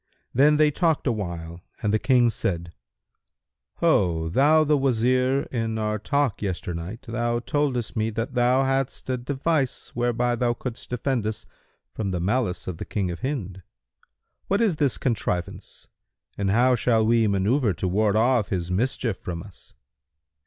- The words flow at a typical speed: Yes, average, 155 wpm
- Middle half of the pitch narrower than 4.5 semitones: No, average, 4.8 semitones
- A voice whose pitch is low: Yes, low, 115 Hz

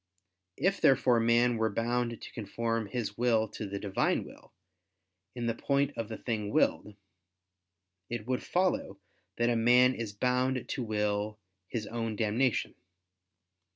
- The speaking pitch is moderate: No, low, 115 Hz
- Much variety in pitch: No, narrow, 2.5 semitones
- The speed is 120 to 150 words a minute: Yes, average, 145 wpm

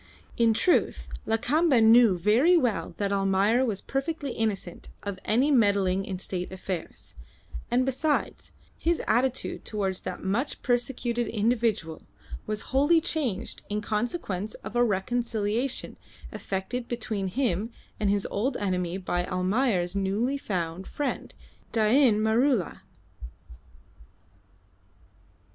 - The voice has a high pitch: Yes, high, 220 Hz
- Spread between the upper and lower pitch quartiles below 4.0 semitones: No, average, 4.3 semitones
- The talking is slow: Yes, slow, 115 wpm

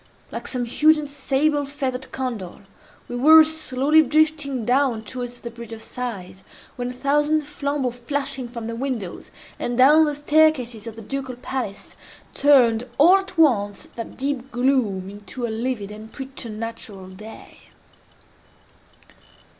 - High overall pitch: Yes, very high, 255 Hz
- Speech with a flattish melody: No, average, 3.9 semitones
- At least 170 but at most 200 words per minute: No, average, 140 wpm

